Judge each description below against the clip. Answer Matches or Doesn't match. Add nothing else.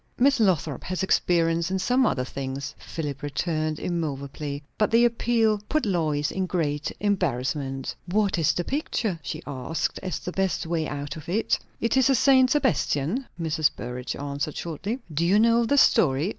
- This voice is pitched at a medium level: Matches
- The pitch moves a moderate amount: Doesn't match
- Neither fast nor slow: Matches